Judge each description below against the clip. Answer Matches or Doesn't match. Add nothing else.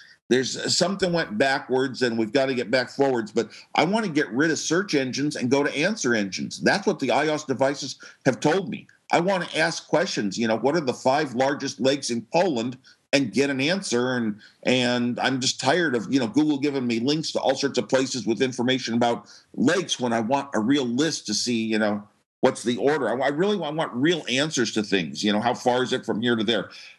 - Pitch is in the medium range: Doesn't match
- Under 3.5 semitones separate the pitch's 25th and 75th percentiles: Matches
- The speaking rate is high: Matches